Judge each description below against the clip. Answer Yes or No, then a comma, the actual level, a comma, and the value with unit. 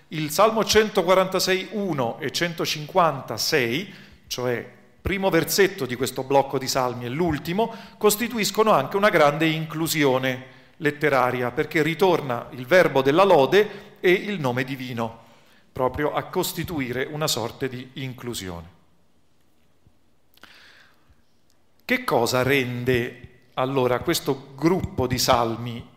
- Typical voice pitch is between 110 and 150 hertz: Yes, medium, 140 Hz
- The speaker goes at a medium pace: No, slow, 105 wpm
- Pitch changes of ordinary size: No, wide, 5.9 semitones